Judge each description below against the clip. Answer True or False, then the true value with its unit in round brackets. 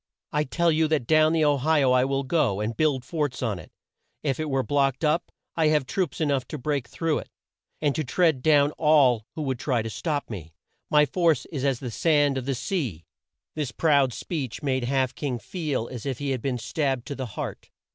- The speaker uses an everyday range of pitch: True (3.4 semitones)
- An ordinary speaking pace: False (225 wpm)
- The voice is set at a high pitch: False (140 Hz)